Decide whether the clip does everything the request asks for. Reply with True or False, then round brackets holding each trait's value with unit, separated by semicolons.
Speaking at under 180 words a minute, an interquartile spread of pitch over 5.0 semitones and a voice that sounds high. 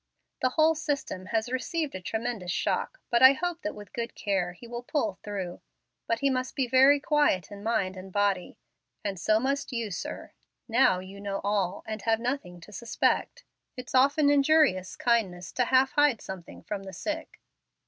False (185 wpm; 5.5 semitones; 230 Hz)